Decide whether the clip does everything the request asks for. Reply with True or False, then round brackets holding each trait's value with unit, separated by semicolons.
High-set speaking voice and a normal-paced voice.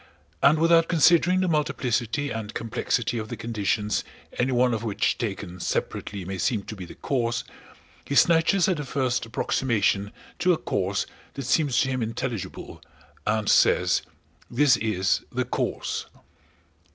False (120 Hz; 150 wpm)